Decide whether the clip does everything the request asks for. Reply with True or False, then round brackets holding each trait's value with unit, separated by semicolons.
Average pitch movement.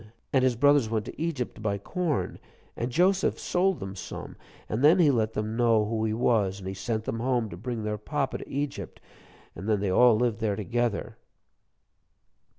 True (3.8 semitones)